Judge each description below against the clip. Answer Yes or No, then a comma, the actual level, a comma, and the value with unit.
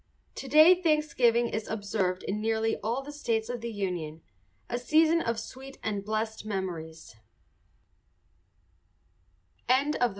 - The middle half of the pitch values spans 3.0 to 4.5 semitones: No, average, 4.9 semitones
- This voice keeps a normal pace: No, slow, 120 wpm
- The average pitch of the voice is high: Yes, high, 225 Hz